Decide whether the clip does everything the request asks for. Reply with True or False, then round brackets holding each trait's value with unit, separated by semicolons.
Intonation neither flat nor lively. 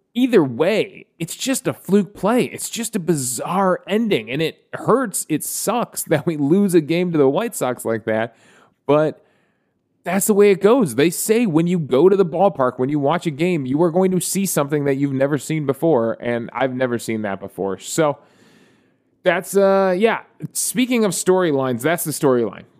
False (6.0 semitones)